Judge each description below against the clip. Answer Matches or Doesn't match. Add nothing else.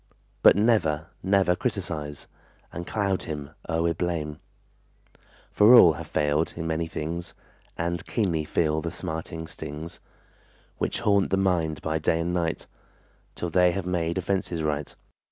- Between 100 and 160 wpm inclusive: Matches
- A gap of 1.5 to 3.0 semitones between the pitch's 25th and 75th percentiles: Matches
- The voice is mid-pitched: Doesn't match